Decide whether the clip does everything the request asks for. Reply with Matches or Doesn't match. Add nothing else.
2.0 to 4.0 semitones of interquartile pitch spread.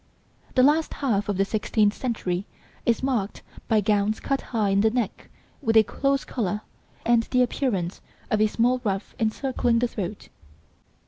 Matches